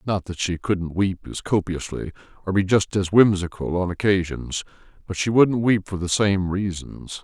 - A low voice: Yes, very low, 95 Hz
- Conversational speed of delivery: Yes, average, 180 wpm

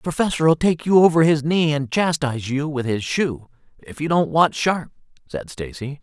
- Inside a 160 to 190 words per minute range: No, average, 200 wpm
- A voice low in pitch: No, medium, 150 Hz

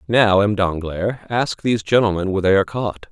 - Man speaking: Yes, male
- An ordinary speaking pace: Yes, average, 190 wpm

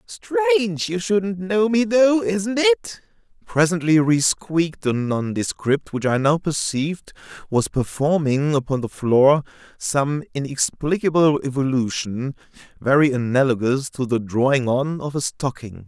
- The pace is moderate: No, slow, 130 wpm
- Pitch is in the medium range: Yes, medium, 155 Hz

